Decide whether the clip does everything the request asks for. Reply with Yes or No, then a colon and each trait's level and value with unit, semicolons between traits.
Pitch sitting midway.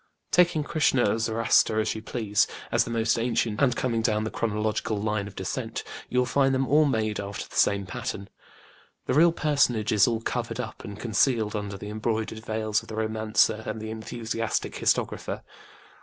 No: low, 110 Hz